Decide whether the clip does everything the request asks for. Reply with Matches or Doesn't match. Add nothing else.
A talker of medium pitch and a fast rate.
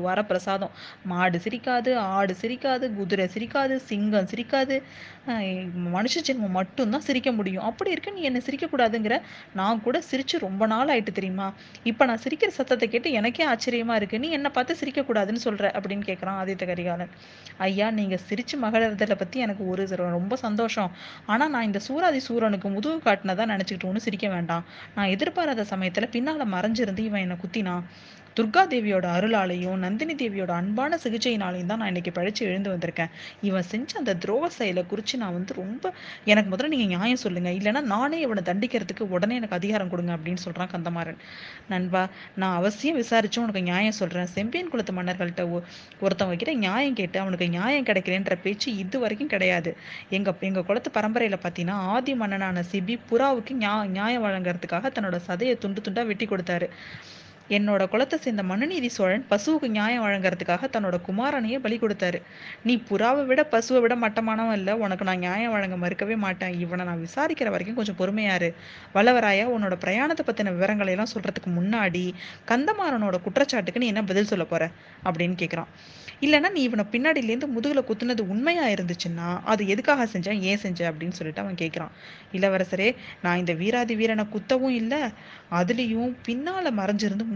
Doesn't match